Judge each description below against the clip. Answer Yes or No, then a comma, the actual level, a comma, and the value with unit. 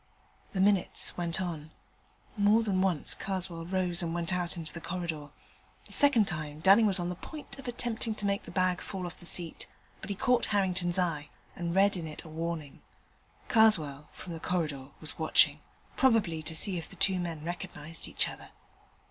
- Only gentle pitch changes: No, average, 3.2 semitones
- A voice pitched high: No, medium, 175 Hz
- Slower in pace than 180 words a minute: No, average, 190 wpm